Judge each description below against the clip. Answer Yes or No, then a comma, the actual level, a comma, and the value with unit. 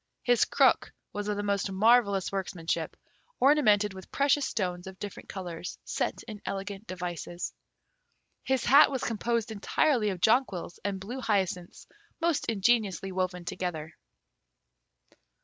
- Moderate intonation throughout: Yes, average, 4.1 semitones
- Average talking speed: No, slow, 130 wpm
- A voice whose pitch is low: No, high, 200 Hz